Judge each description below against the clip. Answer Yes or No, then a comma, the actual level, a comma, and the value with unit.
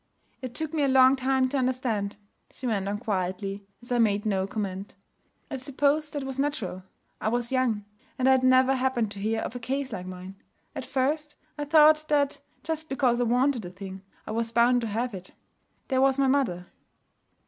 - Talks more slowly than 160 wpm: No, average, 200 wpm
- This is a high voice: Yes, very high, 250 Hz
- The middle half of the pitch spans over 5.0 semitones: No, average, 4.6 semitones